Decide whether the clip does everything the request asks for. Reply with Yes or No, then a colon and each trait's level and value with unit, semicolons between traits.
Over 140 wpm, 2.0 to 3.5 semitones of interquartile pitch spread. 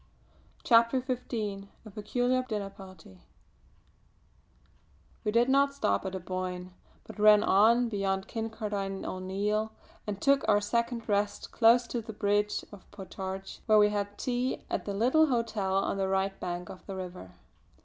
Yes: average, 150 wpm; average, 3.2 semitones